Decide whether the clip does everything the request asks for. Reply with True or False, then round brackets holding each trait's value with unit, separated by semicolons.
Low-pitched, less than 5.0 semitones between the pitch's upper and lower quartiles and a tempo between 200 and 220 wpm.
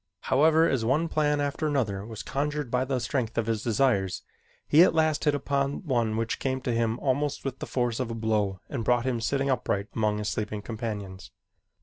True (125 Hz; 4.1 semitones; 205 wpm)